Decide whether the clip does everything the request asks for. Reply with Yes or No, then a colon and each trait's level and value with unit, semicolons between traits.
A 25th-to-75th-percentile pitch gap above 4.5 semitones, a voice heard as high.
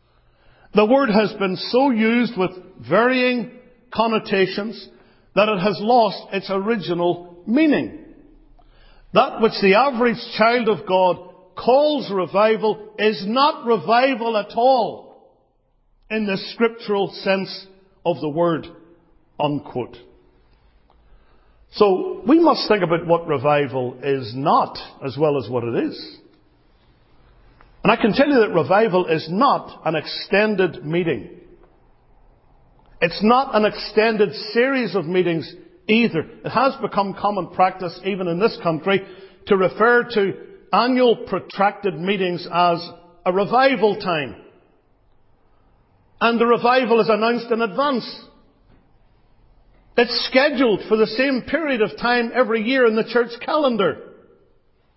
Yes: average, 5.2 semitones; high, 210 Hz